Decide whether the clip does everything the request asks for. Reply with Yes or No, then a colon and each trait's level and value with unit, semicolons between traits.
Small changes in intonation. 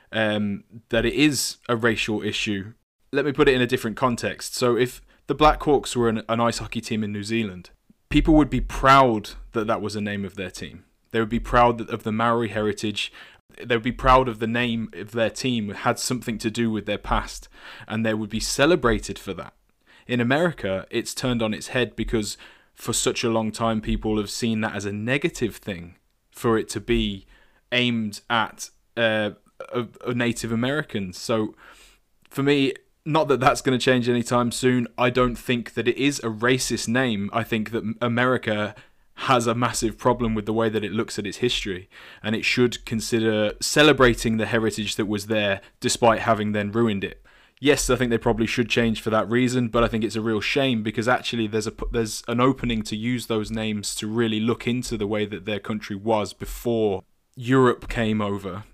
Yes: narrow, 2.3 semitones